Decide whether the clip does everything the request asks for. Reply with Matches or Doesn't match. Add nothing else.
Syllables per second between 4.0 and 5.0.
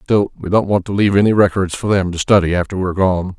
Doesn't match